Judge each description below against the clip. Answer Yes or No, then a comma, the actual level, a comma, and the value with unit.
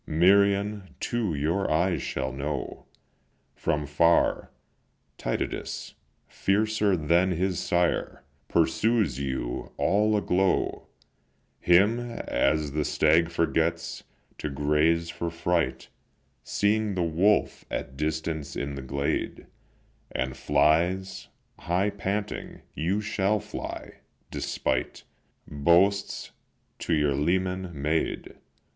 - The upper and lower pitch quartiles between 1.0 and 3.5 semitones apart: No, average, 4.6 semitones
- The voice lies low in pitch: Yes, very low, 85 Hz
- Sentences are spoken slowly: Yes, slow, 100 wpm